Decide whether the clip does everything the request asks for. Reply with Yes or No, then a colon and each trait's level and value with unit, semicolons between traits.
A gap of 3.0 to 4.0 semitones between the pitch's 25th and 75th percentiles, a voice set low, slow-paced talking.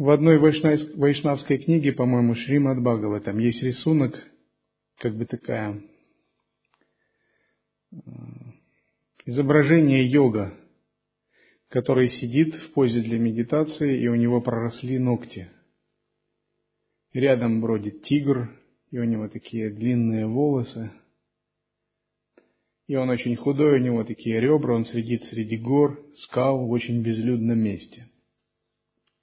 Yes: average, 3.5 semitones; low, 125 Hz; slow, 105 wpm